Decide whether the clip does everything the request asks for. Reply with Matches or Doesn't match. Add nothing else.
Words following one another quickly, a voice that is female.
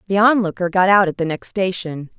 Matches